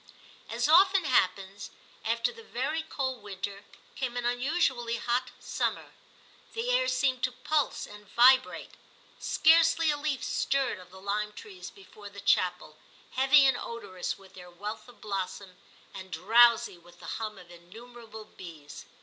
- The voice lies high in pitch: Yes, high, 230 Hz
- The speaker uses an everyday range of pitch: No, wide, 5.7 semitones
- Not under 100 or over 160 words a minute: Yes, average, 150 wpm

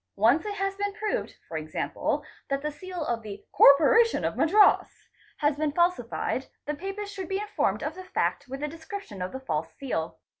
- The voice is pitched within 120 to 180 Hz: No, very high, 300 Hz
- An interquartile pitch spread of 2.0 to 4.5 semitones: No, wide, 7.1 semitones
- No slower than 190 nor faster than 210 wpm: Yes, average, 195 wpm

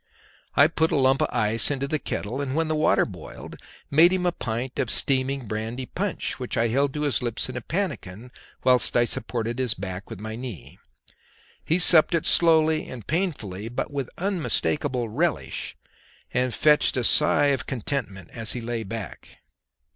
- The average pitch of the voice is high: No, low, 130 Hz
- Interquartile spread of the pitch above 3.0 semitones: Yes, average, 4.8 semitones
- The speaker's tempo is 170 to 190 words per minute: Yes, average, 175 wpm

